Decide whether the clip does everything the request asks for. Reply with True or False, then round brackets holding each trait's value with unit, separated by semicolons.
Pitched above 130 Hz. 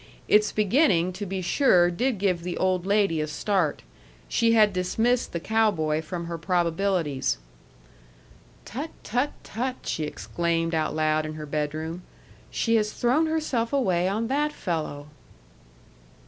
True (185 Hz)